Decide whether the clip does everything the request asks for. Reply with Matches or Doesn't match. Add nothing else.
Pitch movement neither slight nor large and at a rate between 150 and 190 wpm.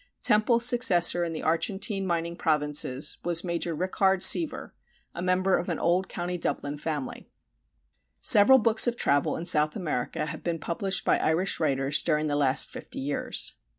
Matches